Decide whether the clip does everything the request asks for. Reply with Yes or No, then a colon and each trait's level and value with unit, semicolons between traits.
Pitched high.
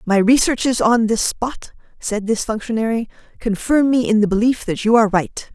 Yes: high, 225 Hz